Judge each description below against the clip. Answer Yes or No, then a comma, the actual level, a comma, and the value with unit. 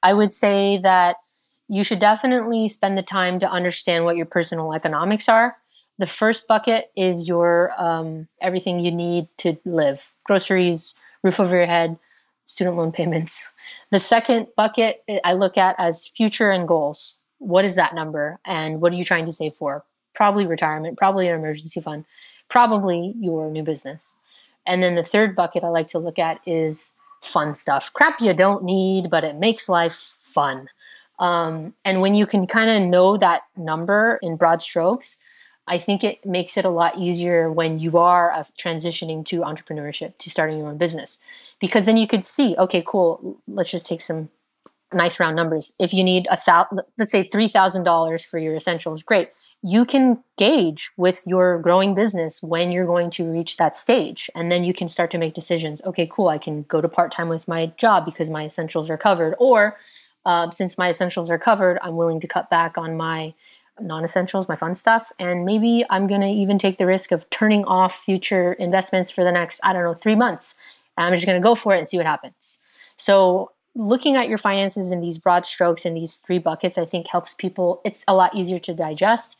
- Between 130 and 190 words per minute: No, average, 200 wpm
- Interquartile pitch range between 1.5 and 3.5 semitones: Yes, average, 3.1 semitones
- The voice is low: No, medium, 180 Hz